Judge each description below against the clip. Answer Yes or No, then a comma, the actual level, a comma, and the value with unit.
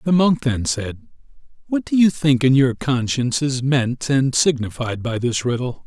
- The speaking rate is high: No, average, 185 wpm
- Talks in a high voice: No, low, 135 Hz